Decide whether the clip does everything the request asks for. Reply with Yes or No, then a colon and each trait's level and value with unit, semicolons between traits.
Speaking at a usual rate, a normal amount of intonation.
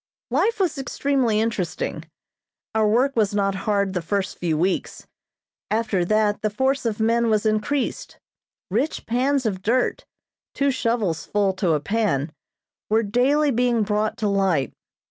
Yes: average, 145 wpm; average, 4.0 semitones